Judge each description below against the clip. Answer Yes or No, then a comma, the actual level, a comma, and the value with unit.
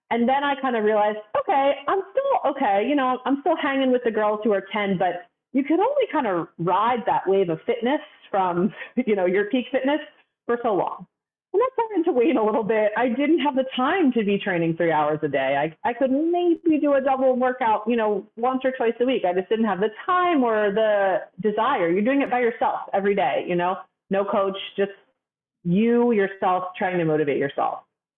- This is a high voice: Yes, high, 230 Hz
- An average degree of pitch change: No, wide, 5.8 semitones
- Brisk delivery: Yes, fast, 220 wpm